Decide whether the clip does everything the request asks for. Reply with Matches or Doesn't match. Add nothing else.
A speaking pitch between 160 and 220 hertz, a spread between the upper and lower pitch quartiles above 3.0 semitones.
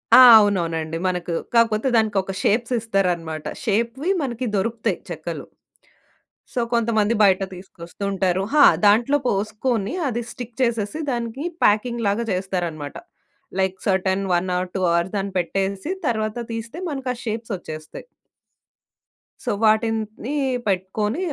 Matches